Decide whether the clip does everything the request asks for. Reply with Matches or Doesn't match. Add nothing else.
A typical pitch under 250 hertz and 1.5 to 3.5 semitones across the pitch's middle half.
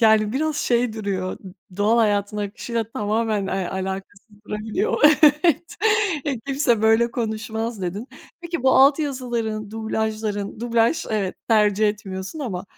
Matches